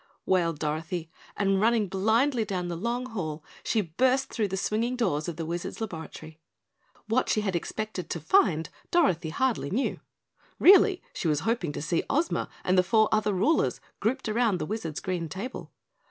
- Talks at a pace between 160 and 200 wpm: Yes, average, 170 wpm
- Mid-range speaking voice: No, high, 195 Hz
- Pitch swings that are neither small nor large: No, wide, 5.9 semitones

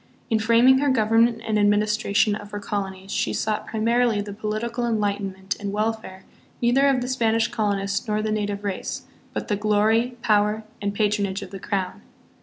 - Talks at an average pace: Yes, average, 175 wpm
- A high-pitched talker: Yes, high, 215 Hz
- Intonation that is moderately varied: No, narrow, 2.0 semitones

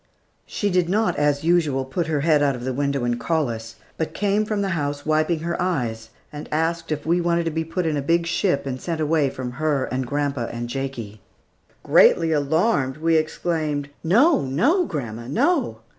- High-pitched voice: No, medium, 155 Hz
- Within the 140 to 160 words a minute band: No, average, 195 wpm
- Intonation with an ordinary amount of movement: Yes, average, 4.0 semitones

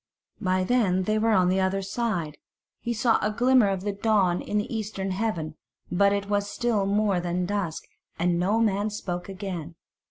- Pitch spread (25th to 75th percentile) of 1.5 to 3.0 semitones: Yes, average, 2.7 semitones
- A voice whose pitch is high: Yes, high, 200 Hz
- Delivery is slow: No, average, 185 wpm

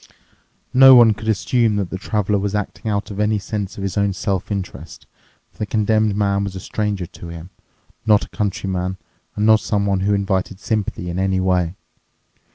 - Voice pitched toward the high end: No, low, 100 Hz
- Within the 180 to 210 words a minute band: Yes, average, 185 wpm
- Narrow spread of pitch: Yes, narrow, 2.0 semitones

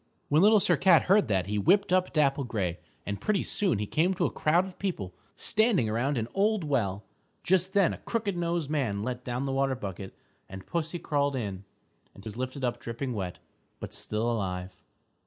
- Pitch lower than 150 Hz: Yes, low, 135 Hz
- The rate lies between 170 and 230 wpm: Yes, average, 200 wpm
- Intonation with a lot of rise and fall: Yes, wide, 9.0 semitones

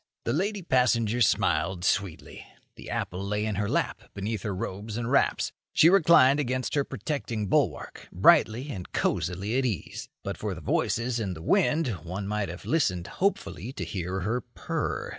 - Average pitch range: No, wide, 5.7 semitones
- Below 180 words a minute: Yes, average, 170 wpm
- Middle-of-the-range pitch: No, low, 110 Hz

